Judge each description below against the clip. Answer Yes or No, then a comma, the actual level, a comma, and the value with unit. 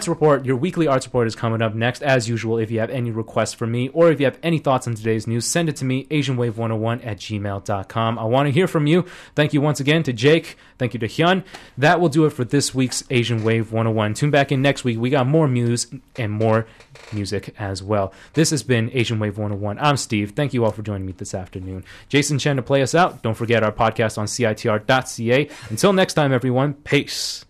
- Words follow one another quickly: Yes, fast, 235 wpm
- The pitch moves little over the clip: No, average, 4.6 semitones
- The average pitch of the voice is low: Yes, low, 125 Hz